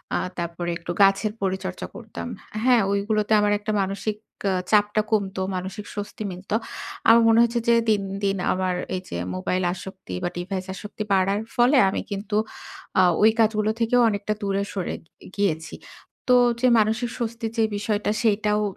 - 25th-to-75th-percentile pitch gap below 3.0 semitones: Yes, narrow, 2.4 semitones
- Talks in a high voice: Yes, high, 205 Hz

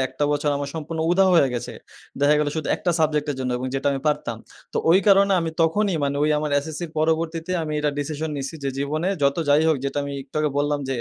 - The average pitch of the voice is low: No, medium, 150 Hz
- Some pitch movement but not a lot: No, narrow, 2.3 semitones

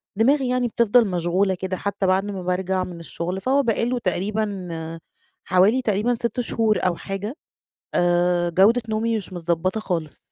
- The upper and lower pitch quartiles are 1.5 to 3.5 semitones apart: No, average, 4.0 semitones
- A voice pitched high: Yes, high, 195 Hz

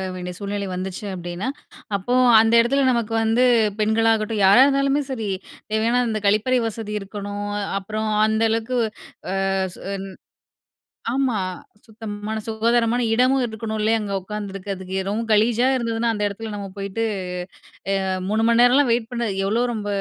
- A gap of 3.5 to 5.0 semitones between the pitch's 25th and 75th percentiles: No, narrow, 2.4 semitones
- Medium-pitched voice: No, high, 220 Hz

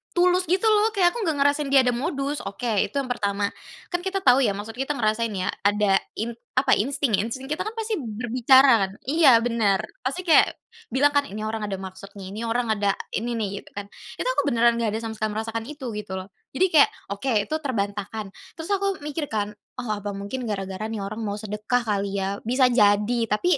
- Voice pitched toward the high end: Yes, high, 230 Hz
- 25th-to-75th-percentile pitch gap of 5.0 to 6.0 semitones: Yes, average, 5.3 semitones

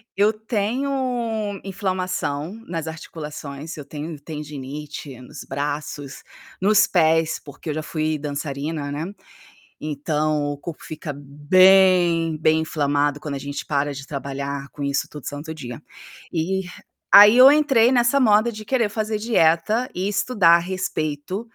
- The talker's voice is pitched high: No, medium, 160 Hz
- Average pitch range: No, wide, 5.8 semitones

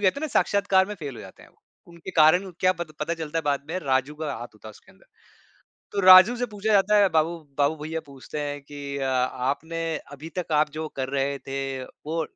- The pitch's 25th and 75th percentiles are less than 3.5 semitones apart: No, average, 4.6 semitones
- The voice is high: No, medium, 155 Hz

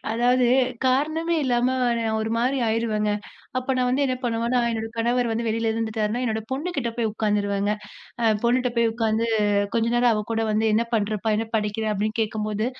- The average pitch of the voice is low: No, high, 230 Hz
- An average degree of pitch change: No, narrow, 2.2 semitones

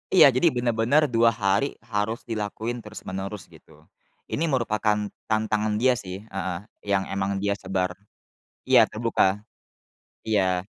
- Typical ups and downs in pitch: Yes, average, 3.0 semitones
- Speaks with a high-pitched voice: No, low, 105 Hz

